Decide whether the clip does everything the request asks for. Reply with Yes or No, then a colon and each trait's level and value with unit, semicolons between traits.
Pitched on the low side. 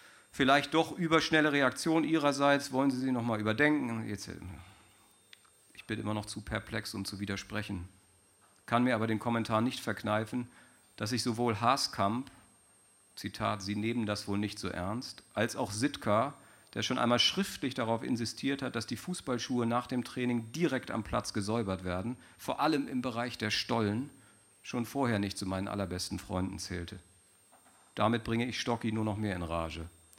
Yes: low, 115 Hz